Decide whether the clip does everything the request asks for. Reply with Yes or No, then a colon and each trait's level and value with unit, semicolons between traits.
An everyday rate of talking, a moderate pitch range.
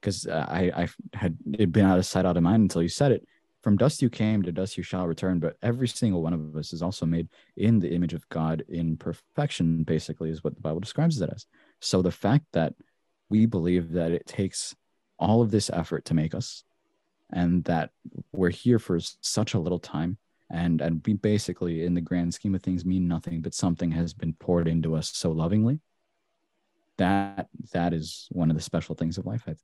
No: fast, 215 wpm; average, 3.7 semitones